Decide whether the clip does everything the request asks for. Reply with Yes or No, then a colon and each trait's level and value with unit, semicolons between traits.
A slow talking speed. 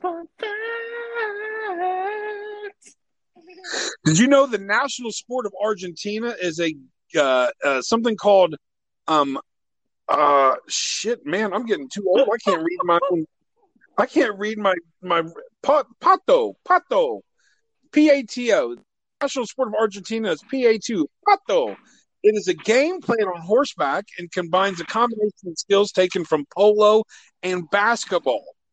Yes: slow, 125 wpm